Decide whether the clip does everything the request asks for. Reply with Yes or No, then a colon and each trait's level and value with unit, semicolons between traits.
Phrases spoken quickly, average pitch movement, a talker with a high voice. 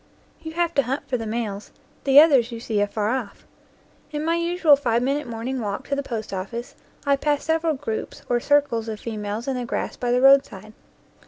Yes: fast, 210 wpm; average, 4.4 semitones; very high, 250 Hz